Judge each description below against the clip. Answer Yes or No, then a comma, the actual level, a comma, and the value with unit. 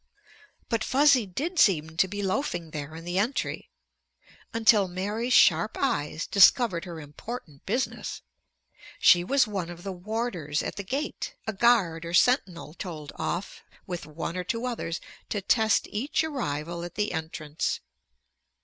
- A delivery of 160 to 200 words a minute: No, average, 150 wpm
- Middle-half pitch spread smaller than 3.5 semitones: No, wide, 5.5 semitones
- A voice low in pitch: No, high, 190 Hz